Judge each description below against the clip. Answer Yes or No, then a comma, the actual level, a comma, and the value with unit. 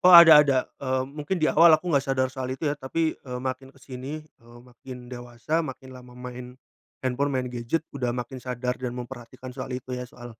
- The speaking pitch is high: No, low, 130 Hz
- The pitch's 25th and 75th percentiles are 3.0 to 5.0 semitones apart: No, narrow, 2.4 semitones